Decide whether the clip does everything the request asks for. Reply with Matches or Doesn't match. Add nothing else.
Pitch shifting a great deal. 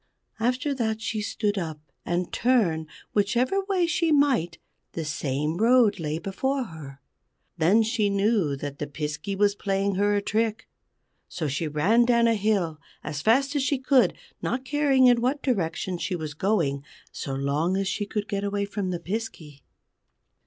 Matches